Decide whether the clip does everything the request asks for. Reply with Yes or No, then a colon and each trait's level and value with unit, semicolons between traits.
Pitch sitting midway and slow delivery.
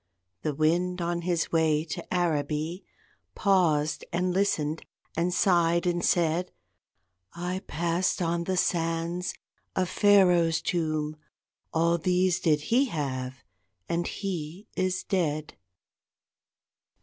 Yes: medium, 170 Hz; slow, 110 wpm